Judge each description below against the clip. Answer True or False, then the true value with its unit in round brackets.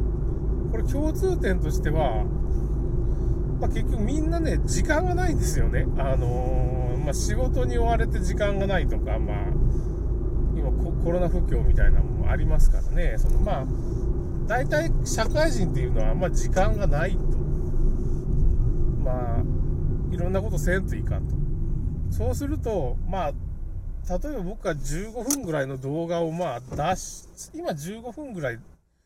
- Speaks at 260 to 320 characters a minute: True (275 characters per minute)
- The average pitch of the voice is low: True (125 Hz)